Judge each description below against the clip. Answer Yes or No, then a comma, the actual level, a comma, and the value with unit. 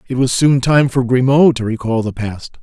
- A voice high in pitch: No, low, 125 Hz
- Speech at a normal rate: No, fast, 230 wpm